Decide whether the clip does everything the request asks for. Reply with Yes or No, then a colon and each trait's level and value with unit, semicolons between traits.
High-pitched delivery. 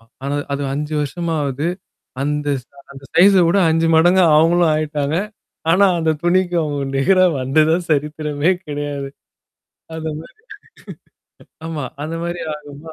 No: medium, 155 Hz